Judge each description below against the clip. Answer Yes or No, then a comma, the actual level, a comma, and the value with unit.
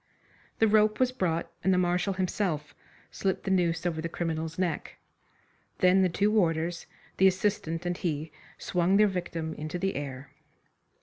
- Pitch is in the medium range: Yes, medium, 175 Hz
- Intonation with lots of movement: No, average, 2.8 semitones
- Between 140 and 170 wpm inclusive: Yes, average, 160 wpm